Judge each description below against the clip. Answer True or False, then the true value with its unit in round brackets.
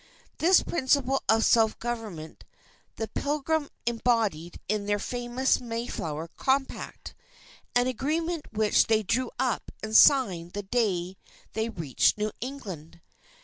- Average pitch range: True (4.5 semitones)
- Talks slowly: True (120 wpm)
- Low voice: False (230 Hz)